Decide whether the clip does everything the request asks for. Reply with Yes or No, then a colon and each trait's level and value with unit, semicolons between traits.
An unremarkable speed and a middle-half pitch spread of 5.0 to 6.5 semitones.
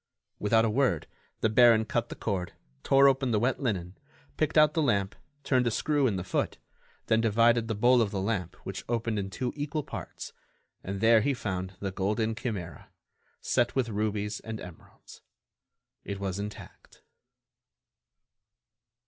No: average, 160 wpm; average, 3.6 semitones